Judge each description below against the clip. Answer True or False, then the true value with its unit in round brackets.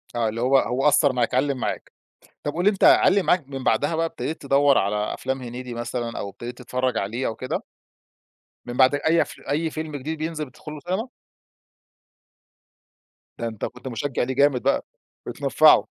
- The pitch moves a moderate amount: True (3.6 semitones)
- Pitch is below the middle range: True (130 Hz)